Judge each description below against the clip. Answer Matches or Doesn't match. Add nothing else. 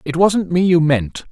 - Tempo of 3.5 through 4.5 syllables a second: Matches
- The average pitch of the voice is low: Doesn't match